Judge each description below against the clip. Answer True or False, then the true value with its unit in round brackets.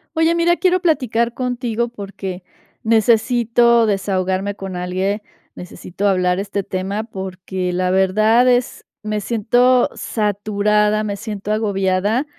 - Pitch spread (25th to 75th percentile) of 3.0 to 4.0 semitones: True (3.6 semitones)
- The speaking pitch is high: True (210 Hz)